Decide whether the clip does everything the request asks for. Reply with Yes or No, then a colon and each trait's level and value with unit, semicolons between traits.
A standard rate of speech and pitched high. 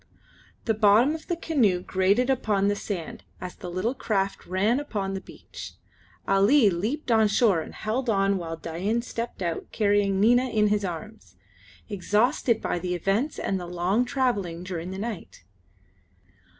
Yes: average, 160 wpm; high, 205 Hz